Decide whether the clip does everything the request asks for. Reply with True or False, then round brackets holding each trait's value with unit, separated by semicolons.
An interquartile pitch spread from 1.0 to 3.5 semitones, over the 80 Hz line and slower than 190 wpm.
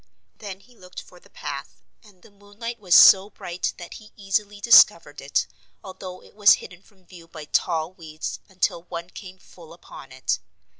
True (2.9 semitones; 185 Hz; 180 wpm)